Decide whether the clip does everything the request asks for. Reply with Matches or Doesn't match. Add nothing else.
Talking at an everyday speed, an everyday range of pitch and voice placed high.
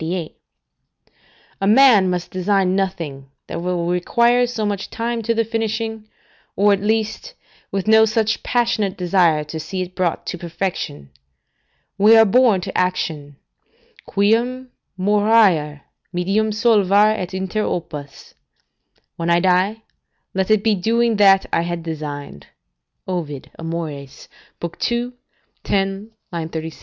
Doesn't match